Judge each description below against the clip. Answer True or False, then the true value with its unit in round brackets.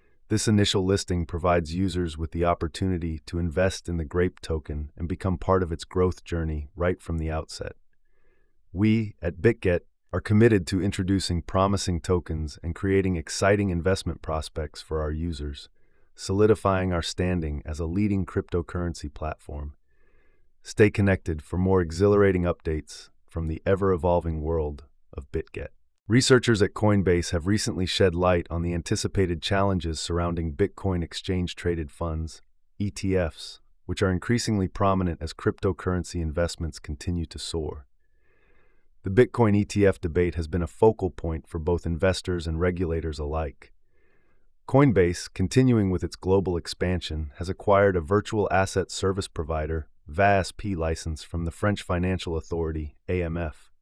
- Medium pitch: False (90 Hz)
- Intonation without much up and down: False (3.1 semitones)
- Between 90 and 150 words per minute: True (140 wpm)